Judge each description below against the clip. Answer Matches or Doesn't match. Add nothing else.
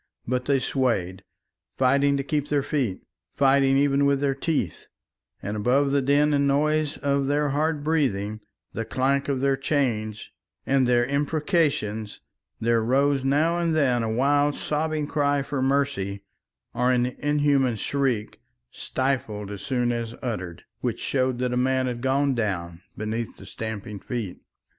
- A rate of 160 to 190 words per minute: Doesn't match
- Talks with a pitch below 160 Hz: Matches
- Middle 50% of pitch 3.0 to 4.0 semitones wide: Matches